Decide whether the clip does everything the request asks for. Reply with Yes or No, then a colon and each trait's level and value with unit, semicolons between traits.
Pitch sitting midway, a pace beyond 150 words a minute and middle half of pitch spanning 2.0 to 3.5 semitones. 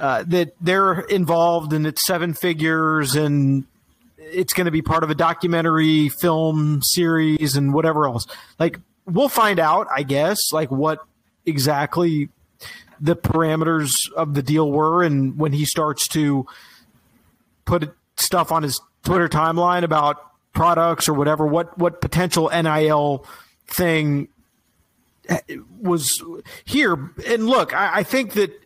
No: medium, 160 Hz; slow, 135 wpm; average, 2.7 semitones